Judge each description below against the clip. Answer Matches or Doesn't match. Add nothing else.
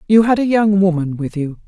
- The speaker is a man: Doesn't match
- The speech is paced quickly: Matches